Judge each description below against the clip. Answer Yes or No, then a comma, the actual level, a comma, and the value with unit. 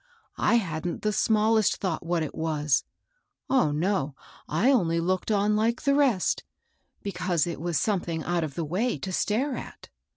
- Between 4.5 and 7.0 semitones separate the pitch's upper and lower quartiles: Yes, average, 5.1 semitones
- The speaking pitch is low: No, medium, 185 Hz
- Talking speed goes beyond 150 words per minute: Yes, average, 170 wpm